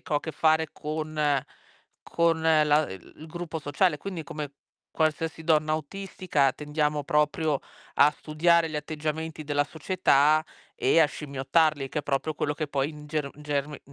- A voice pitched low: No, medium, 155 Hz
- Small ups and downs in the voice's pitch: Yes, narrow, 1.5 semitones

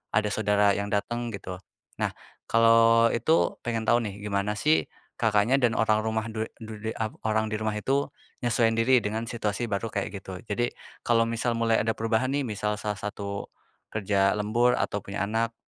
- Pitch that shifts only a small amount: Yes, narrow, 1.9 semitones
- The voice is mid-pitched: No, low, 110 Hz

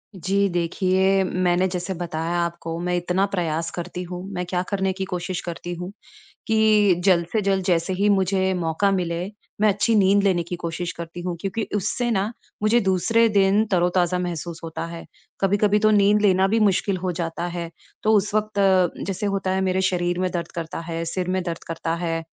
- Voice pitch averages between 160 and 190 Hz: Yes, medium, 185 Hz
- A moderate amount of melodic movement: No, narrow, 2.3 semitones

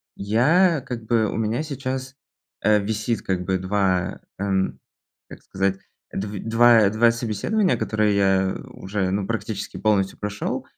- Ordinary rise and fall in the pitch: Yes, average, 3.2 semitones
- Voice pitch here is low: Yes, low, 105 Hz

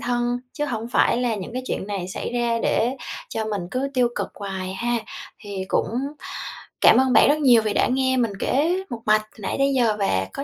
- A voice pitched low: No, high, 235 Hz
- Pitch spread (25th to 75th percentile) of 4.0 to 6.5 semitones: No, average, 3.6 semitones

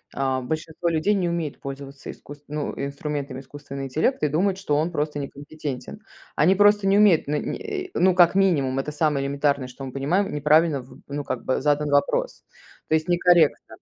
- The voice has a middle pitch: Yes, medium, 150 Hz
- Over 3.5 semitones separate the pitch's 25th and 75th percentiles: Yes, average, 4.0 semitones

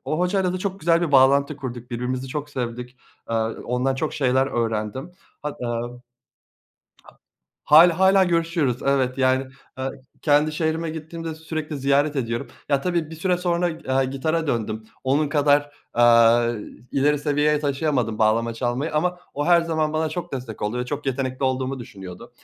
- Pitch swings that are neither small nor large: Yes, average, 4.2 semitones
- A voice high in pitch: No, medium, 140 Hz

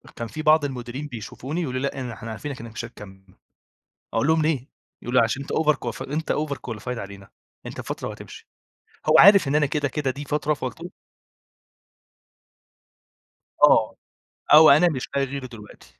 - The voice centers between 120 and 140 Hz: Yes, low, 135 Hz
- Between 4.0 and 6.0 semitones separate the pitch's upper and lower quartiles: Yes, average, 4.4 semitones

